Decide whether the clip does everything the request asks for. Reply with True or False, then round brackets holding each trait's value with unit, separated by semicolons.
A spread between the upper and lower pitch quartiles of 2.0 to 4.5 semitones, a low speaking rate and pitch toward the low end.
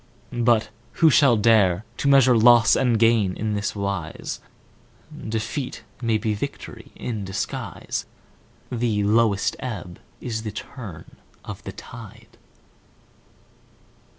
True (2.7 semitones; 115 wpm; 110 Hz)